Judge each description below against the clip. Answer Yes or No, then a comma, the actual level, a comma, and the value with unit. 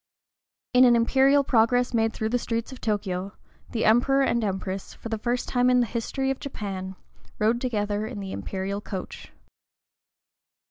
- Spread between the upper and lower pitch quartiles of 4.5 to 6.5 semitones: No, average, 3.3 semitones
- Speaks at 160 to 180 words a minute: Yes, average, 165 wpm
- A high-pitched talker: Yes, high, 230 Hz